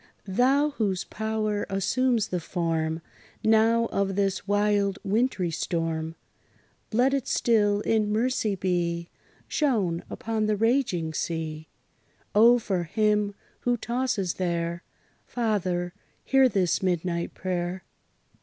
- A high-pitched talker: Yes, high, 200 Hz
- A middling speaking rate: No, slow, 110 wpm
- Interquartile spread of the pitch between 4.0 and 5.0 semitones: Yes, average, 4.3 semitones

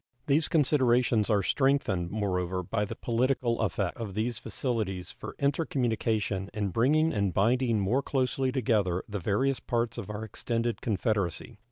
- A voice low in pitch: Yes, low, 115 Hz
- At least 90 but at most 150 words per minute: Yes, average, 145 wpm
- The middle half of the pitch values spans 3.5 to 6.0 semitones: Yes, average, 4.3 semitones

